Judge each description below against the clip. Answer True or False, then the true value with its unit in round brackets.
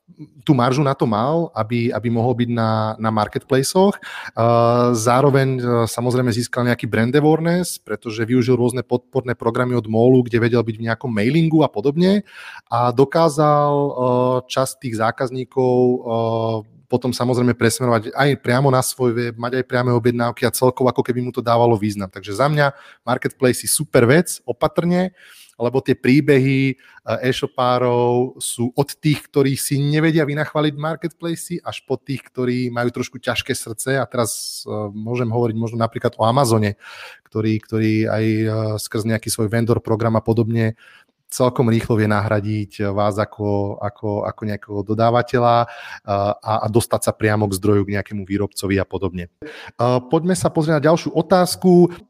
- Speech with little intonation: False (3.2 semitones)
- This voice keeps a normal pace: True (155 wpm)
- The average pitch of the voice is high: False (120 Hz)